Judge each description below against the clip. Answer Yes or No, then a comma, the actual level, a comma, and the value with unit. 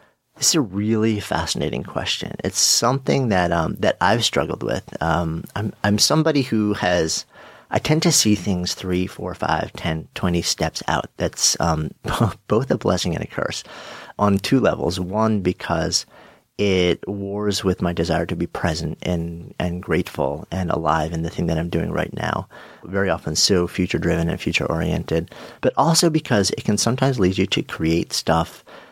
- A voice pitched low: Yes, very low, 95 Hz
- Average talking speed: Yes, average, 175 wpm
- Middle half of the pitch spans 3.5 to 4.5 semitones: Yes, average, 4.1 semitones